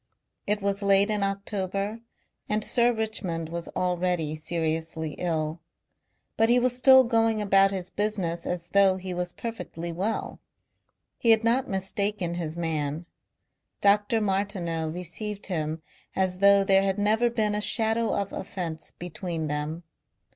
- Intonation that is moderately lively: Yes, average, 3.8 semitones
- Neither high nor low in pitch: No, high, 195 Hz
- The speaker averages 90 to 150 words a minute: Yes, average, 140 wpm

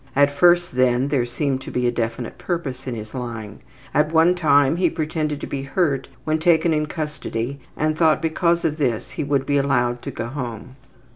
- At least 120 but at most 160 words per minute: No, average, 200 wpm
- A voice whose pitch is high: No, medium, 140 Hz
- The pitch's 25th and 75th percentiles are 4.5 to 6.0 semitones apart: No, average, 4.1 semitones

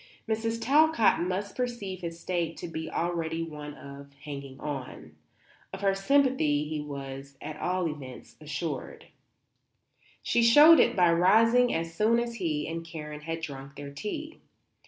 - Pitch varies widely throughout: Yes, wide, 6.4 semitones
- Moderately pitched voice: Yes, medium, 165 Hz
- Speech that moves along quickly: No, average, 150 wpm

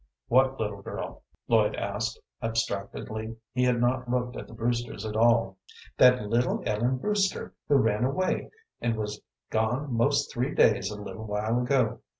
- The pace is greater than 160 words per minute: No, average, 155 wpm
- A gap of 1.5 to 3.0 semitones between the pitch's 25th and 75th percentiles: Yes, average, 2.7 semitones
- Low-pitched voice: Yes, low, 115 Hz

